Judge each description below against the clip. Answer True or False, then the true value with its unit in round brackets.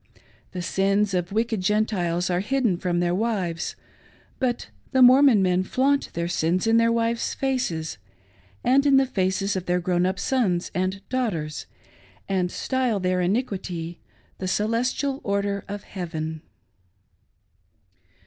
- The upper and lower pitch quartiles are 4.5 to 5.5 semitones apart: True (4.8 semitones)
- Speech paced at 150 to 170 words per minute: False (140 wpm)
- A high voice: True (195 Hz)